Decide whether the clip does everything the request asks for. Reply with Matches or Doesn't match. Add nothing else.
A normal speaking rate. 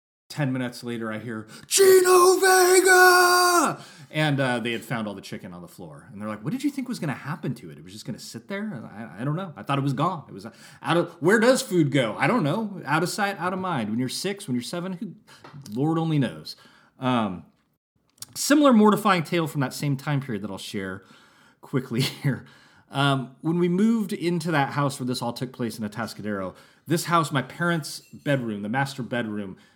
Doesn't match